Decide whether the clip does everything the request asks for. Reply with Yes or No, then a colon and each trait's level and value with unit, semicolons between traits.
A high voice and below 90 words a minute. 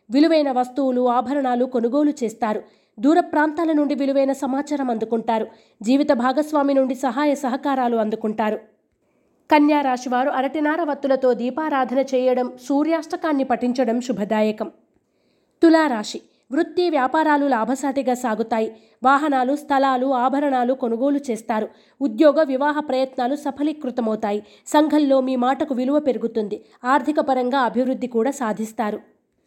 No: very high, 265 Hz; average, 100 wpm